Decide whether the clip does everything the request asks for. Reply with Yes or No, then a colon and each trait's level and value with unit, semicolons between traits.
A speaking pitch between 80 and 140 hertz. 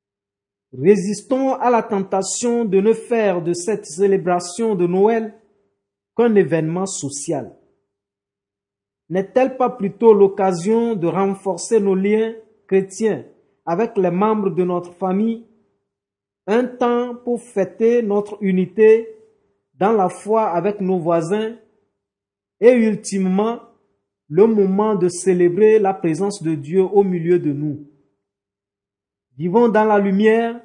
No: high, 195 Hz